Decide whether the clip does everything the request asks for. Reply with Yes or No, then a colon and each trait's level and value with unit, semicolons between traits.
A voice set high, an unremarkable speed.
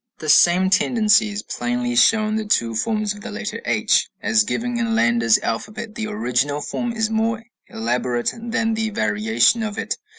Yes: high, 205 Hz; average, 175 wpm